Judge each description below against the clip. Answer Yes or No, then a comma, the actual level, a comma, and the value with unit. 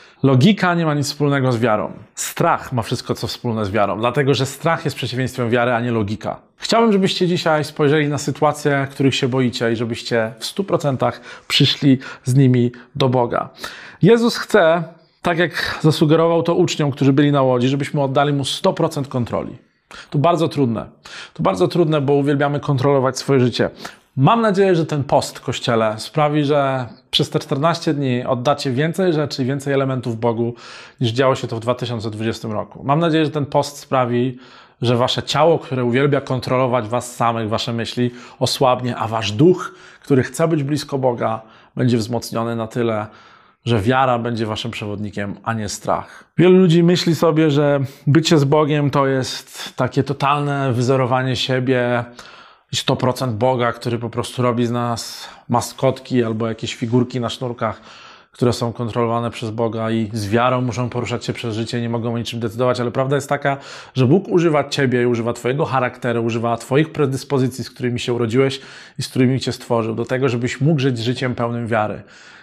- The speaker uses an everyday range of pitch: Yes, average, 3.4 semitones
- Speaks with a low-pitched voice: Yes, low, 130 Hz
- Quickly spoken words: Yes, fast, 175 wpm